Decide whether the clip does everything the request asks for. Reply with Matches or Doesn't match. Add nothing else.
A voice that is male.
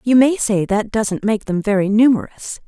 Doesn't match